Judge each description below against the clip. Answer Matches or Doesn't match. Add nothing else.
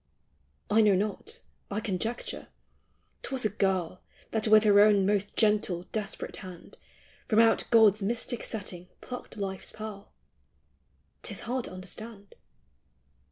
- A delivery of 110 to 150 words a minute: Matches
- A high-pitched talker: Matches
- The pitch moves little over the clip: Matches